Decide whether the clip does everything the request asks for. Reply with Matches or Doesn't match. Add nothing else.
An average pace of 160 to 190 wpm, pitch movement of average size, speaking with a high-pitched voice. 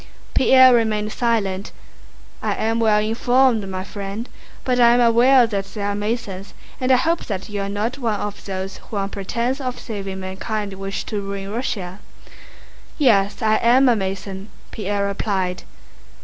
Matches